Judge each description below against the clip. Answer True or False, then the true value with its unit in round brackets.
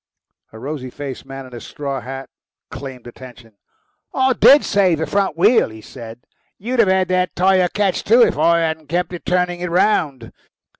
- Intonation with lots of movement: True (6.0 semitones)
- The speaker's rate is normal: True (180 wpm)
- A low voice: False (165 Hz)